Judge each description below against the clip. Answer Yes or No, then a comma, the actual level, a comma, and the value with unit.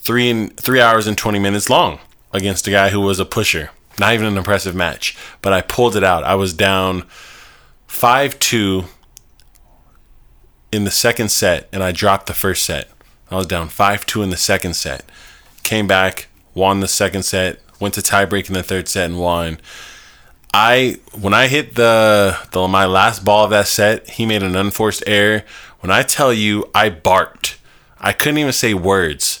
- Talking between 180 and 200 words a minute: Yes, average, 190 wpm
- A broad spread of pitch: No, narrow, 2.4 semitones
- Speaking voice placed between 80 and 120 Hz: Yes, low, 100 Hz